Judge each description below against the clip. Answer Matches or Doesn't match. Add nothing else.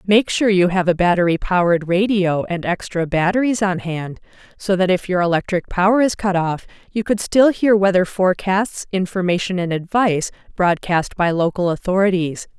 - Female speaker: Matches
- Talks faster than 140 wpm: Matches